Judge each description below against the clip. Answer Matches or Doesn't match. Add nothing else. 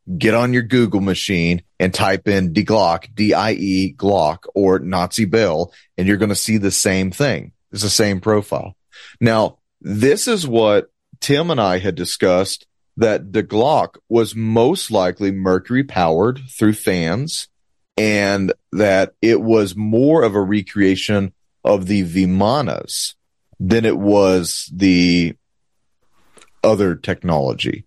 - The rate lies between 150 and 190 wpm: Doesn't match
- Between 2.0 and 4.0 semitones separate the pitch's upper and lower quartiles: Matches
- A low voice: Matches